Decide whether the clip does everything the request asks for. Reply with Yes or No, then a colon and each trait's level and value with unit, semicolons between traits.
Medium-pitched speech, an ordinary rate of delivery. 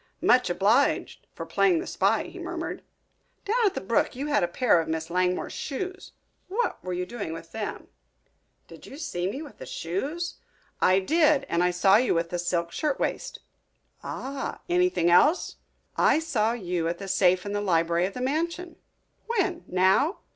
No: high, 210 Hz; average, 175 wpm